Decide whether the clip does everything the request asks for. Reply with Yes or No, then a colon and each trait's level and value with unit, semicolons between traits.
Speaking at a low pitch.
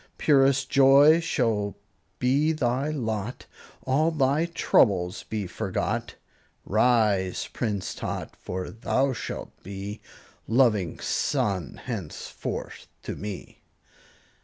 Yes: low, 120 Hz